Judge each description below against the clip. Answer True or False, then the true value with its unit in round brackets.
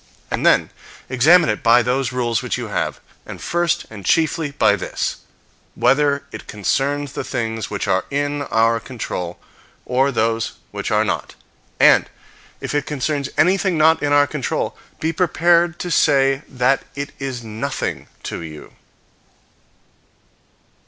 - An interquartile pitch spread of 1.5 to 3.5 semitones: False (4.4 semitones)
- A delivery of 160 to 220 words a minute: False (145 wpm)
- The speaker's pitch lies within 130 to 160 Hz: True (135 Hz)